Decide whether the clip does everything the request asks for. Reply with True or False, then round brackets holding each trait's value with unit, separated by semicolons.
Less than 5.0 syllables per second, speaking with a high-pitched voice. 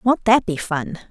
True (4.1 syllables/s; 195 Hz)